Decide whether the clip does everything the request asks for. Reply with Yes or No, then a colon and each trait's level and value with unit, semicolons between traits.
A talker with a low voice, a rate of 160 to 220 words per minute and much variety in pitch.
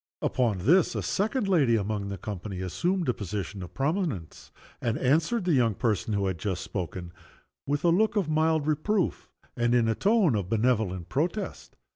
Yes: low, 120 Hz; average, 175 wpm; wide, 8.8 semitones